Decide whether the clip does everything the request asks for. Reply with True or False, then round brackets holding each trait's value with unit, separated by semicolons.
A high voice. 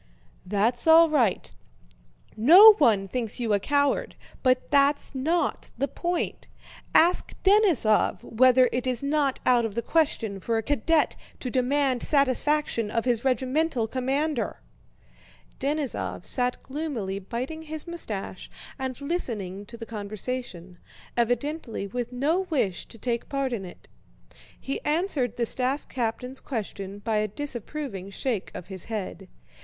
True (255 Hz)